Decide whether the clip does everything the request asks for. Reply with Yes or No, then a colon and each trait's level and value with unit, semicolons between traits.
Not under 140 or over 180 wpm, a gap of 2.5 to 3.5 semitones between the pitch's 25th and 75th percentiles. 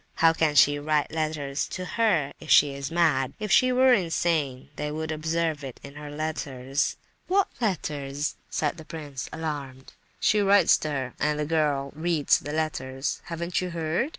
Yes: average, 165 wpm; average, 2.9 semitones